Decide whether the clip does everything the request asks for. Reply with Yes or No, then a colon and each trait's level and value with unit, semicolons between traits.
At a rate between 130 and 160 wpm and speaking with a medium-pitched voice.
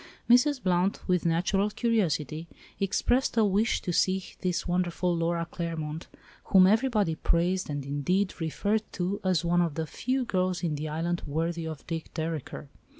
Yes: average, 150 wpm; medium, 175 Hz